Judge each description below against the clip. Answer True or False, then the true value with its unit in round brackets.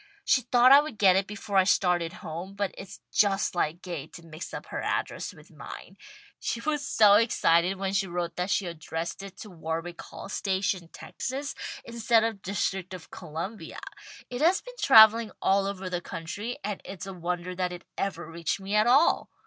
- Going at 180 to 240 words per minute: True (190 wpm)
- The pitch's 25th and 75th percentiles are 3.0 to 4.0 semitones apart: True (3.6 semitones)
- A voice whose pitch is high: True (195 Hz)